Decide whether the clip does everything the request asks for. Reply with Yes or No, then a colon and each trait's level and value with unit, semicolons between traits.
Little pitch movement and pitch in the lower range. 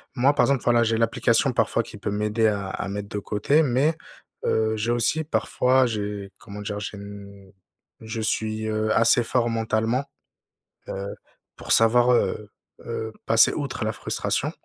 Yes: narrow, 2.3 semitones; low, 110 Hz